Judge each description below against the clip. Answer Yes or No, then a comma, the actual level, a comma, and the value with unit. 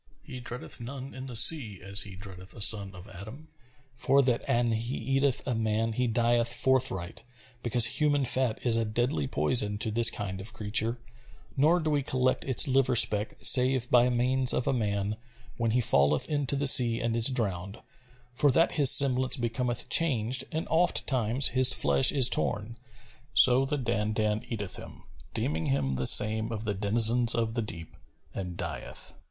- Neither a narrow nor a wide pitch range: Yes, average, 3.6 semitones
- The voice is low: Yes, low, 120 Hz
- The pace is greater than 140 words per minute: Yes, average, 175 wpm